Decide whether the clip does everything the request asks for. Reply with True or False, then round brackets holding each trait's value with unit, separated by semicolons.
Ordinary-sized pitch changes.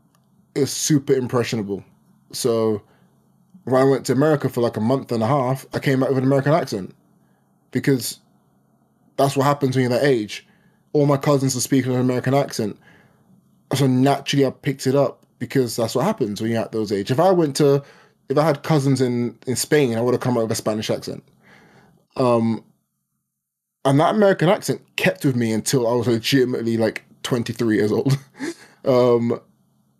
True (3.4 semitones)